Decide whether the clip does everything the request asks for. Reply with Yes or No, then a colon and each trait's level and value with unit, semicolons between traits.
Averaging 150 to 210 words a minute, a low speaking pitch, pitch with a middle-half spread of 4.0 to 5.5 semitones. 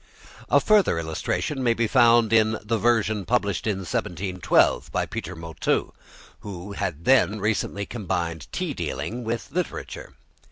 No: slow, 135 wpm; low, 105 Hz; average, 4.3 semitones